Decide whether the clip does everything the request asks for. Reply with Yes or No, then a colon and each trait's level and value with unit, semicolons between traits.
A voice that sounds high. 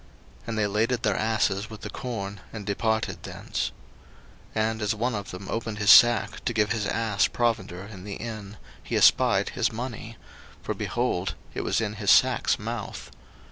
No: low, 110 Hz